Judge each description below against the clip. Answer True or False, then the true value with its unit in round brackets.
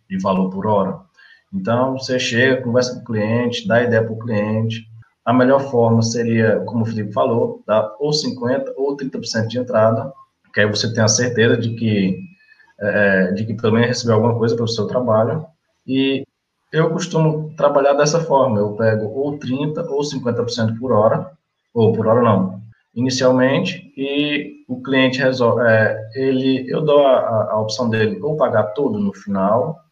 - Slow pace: False (170 wpm)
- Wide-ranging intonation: False (3.8 semitones)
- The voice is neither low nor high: False (120 Hz)